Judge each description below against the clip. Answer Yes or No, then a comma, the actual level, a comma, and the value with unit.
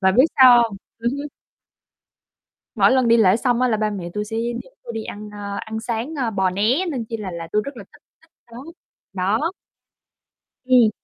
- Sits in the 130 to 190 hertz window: No, high, 225 Hz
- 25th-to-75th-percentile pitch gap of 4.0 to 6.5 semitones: No, average, 3.5 semitones